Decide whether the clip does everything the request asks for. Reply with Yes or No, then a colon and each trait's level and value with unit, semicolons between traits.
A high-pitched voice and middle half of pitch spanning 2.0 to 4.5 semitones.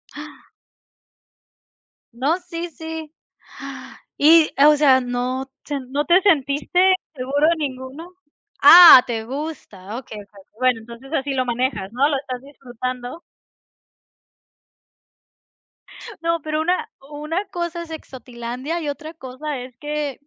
Yes: very high, 280 Hz; average, 4.0 semitones